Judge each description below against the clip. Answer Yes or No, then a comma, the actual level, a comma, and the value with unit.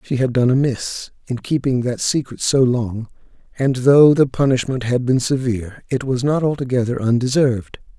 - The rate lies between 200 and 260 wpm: No, average, 165 wpm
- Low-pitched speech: Yes, low, 130 Hz